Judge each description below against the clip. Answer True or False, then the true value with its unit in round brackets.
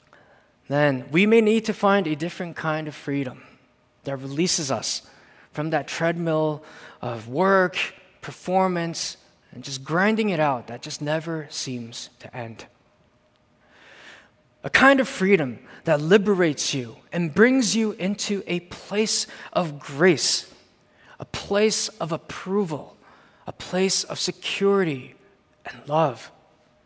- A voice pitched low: False (165 Hz)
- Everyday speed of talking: False (125 wpm)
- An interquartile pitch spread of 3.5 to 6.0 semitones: True (5.5 semitones)